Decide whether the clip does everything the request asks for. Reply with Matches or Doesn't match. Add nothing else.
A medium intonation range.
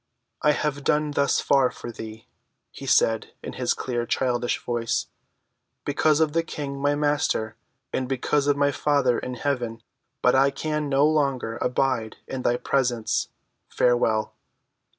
Matches